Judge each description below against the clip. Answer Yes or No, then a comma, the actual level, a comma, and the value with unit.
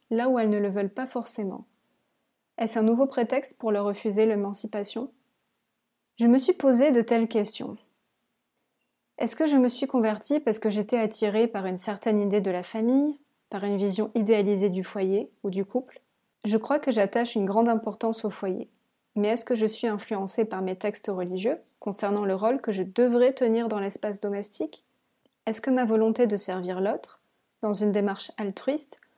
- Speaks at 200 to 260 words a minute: No, average, 185 wpm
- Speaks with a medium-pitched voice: No, high, 220 Hz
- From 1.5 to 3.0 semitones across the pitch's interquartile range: Yes, average, 2.7 semitones